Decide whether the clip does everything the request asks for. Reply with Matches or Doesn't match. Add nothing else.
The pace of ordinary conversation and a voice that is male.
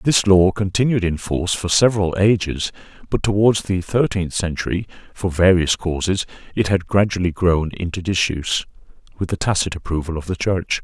Matches